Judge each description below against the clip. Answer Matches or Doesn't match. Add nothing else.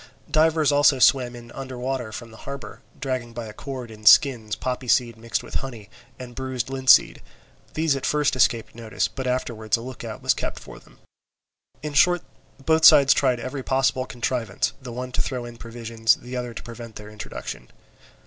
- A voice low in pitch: Matches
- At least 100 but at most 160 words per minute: Doesn't match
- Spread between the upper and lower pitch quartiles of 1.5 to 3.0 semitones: Matches